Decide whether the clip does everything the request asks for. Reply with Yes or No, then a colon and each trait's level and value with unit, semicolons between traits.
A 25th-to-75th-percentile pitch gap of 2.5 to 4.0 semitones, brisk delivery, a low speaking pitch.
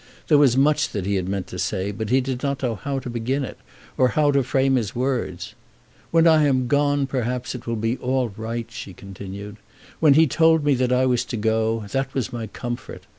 Yes: average, 3.5 semitones; fast, 220 wpm; low, 125 Hz